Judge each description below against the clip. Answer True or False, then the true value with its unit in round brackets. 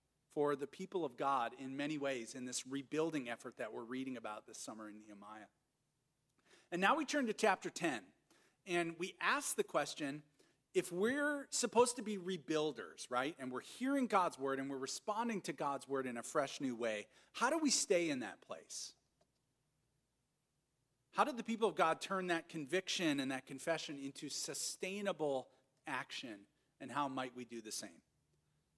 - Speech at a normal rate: True (175 wpm)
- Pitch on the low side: False (150 Hz)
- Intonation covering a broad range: True (6.5 semitones)